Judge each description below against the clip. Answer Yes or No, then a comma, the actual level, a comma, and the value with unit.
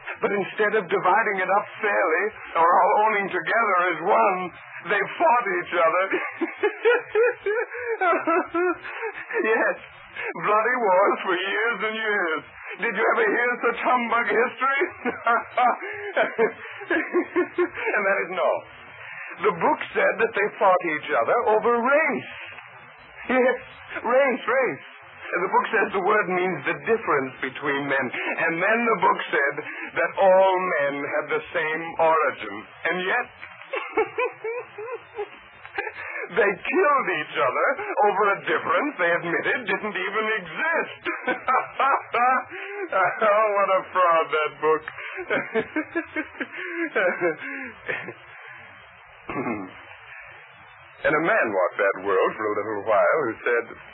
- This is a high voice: Yes, high, 235 Hz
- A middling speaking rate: No, slow, 115 wpm